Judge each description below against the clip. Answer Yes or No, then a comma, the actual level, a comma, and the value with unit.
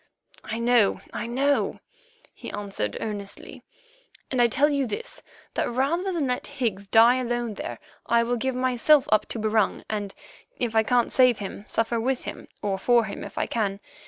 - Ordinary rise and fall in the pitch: Yes, average, 3.2 semitones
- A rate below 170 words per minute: No, average, 180 wpm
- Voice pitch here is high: Yes, high, 235 Hz